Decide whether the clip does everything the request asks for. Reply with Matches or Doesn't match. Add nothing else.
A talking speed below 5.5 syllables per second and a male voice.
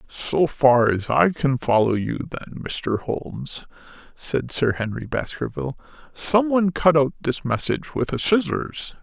Matches